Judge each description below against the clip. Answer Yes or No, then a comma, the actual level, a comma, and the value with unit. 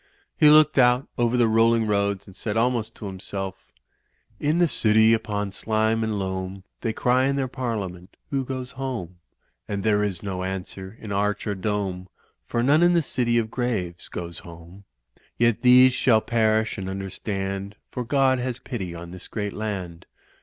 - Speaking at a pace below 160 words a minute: No, average, 175 wpm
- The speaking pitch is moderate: No, low, 110 Hz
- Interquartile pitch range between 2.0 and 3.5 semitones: No, average, 4.2 semitones